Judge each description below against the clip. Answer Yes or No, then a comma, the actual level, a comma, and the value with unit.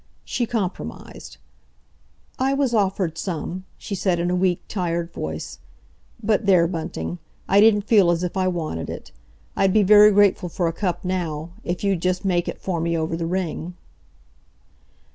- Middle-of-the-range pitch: Yes, medium, 180 Hz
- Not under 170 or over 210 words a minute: No, average, 160 wpm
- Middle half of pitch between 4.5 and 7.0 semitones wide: No, average, 2.8 semitones